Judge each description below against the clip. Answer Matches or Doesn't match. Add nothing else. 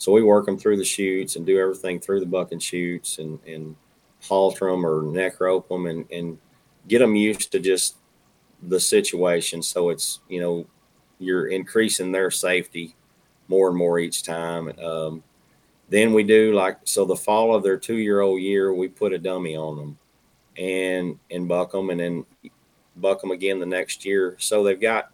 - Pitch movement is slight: Matches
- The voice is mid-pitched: Doesn't match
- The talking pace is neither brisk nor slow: Matches